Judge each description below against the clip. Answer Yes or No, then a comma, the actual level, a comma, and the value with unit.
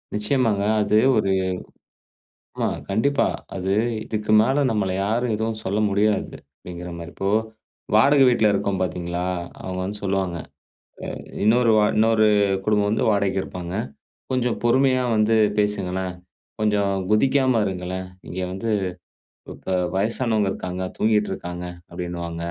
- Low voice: Yes, low, 105 Hz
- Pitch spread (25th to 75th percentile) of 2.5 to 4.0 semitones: Yes, average, 3.2 semitones